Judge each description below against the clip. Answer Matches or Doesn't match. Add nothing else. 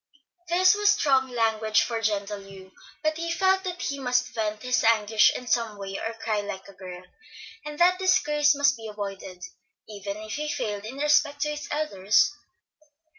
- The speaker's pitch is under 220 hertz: Doesn't match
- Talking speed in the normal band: Matches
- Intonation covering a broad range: Matches